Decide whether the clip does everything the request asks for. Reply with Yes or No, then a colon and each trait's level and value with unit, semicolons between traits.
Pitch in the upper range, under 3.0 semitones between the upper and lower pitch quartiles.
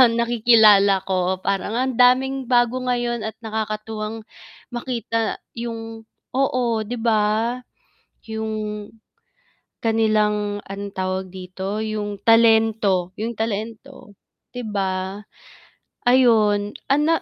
Yes: high, 220 Hz; narrow, 2.4 semitones